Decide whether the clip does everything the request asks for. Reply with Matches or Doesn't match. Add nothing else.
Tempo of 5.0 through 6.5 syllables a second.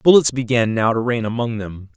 Matches